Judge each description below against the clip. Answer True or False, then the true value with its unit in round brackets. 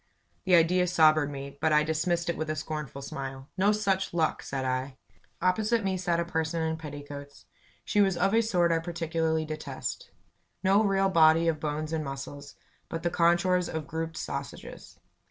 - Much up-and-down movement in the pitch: False (3.0 semitones)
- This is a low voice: False (160 Hz)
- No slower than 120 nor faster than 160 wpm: False (175 wpm)